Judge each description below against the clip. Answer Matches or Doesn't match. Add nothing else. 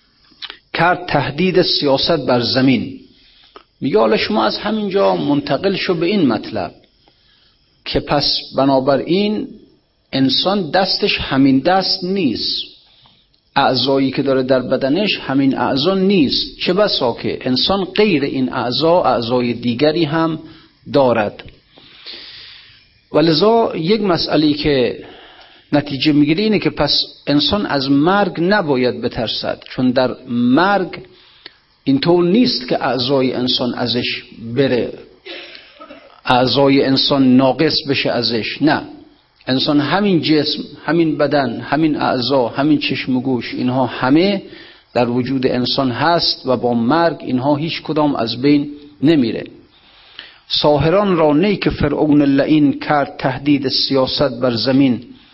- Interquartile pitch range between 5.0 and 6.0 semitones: Matches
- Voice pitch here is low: Doesn't match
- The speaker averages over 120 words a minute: Doesn't match